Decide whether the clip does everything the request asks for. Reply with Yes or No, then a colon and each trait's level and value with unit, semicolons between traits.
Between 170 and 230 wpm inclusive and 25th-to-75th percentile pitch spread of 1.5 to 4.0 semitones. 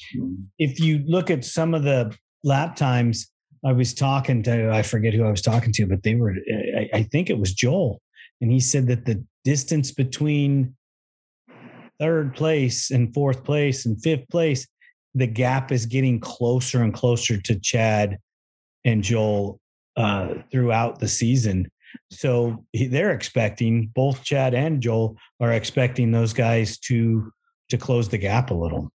No: average, 155 wpm; average, 3.3 semitones